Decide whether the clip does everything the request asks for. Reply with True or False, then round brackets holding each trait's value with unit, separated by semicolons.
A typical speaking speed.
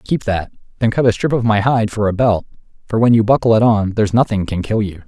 False (270 wpm)